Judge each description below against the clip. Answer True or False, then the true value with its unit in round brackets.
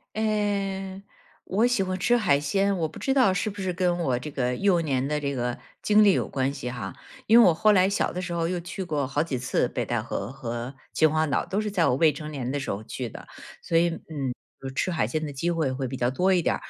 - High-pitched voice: False (165 Hz)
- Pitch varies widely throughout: True (6.1 semitones)